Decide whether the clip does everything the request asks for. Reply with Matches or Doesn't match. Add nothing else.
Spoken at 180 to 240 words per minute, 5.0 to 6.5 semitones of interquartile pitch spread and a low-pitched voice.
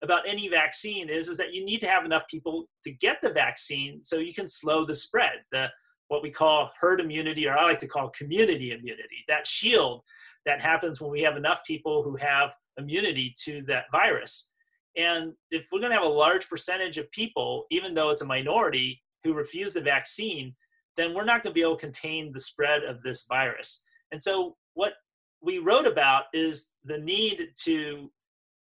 Doesn't match